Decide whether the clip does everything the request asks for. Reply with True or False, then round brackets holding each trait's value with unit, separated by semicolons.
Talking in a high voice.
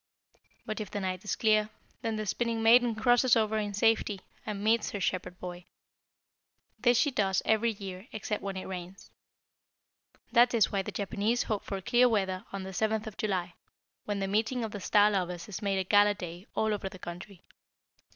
True (205 Hz)